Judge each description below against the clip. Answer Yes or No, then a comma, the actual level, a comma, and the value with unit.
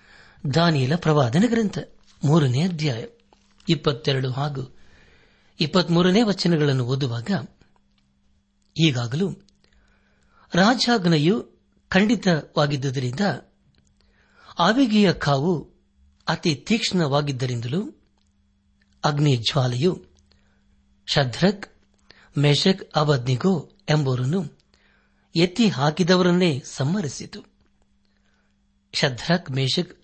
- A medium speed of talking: No, slow, 50 wpm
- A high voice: No, medium, 150 Hz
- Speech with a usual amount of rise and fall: No, wide, 6.1 semitones